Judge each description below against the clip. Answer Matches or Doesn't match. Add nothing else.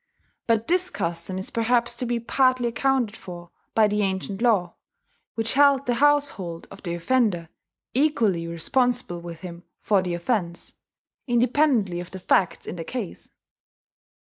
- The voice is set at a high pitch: Matches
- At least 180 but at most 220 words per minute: Doesn't match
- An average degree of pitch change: Doesn't match